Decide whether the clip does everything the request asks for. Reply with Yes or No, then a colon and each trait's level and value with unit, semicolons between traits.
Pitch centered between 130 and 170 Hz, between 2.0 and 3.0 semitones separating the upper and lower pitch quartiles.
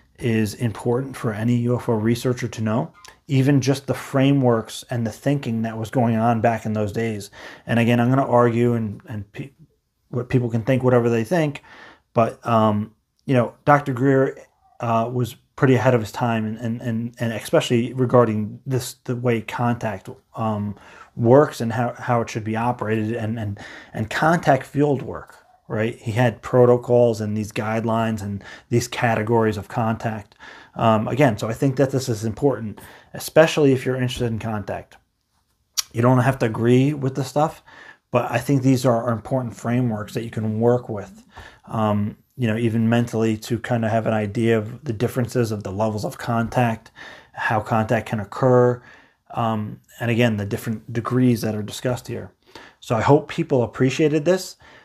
No: low, 120 Hz; narrow, 2.4 semitones